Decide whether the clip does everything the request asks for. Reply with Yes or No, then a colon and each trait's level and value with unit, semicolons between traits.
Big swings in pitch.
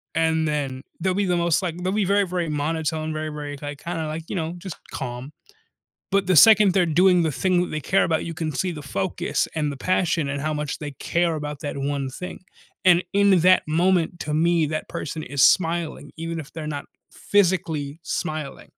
No: average, 3.1 semitones